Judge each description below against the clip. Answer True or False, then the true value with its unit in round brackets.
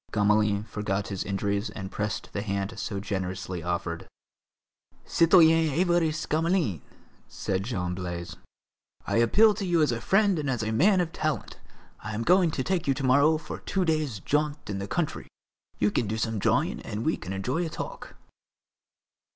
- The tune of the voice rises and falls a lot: True (8.4 semitones)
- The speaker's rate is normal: True (175 wpm)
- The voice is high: False (115 Hz)